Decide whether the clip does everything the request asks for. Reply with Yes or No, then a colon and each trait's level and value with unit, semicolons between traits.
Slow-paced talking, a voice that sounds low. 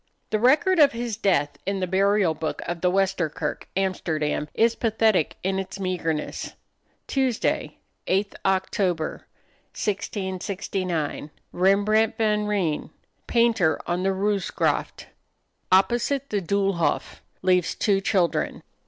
No: slow, 115 wpm; high, 195 Hz